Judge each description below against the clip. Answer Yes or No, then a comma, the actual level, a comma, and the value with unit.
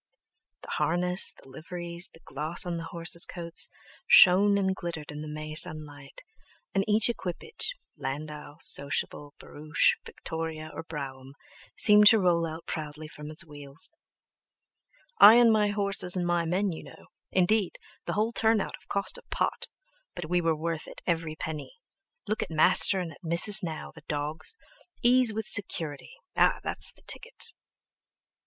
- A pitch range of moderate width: Yes, average, 4.4 semitones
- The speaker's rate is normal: Yes, average, 155 wpm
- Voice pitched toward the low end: No, medium, 170 Hz